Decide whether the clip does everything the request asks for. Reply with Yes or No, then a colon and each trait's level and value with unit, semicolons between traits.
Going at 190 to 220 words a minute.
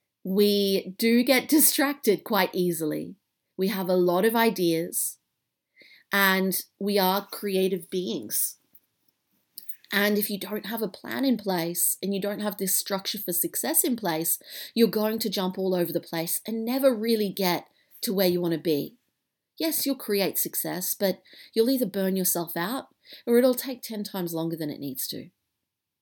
No: average, 170 wpm